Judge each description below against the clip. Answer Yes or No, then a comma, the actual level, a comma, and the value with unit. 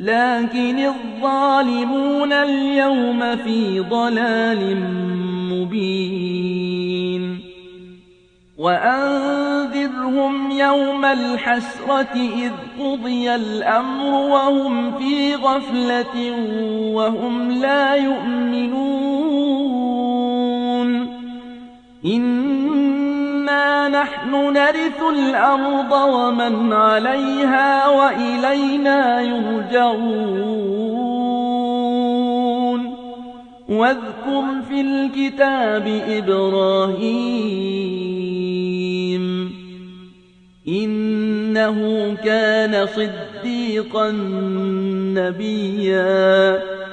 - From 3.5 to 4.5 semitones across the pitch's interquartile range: No, average, 4.9 semitones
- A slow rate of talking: Yes, slow, 45 wpm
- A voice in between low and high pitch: No, high, 245 Hz